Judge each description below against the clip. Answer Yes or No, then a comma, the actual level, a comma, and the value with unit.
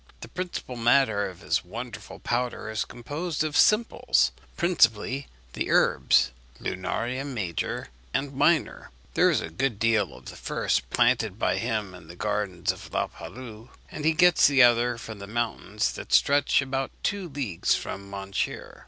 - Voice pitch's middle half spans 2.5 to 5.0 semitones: No, wide, 5.4 semitones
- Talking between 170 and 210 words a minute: No, average, 160 wpm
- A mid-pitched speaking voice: No, low, 120 Hz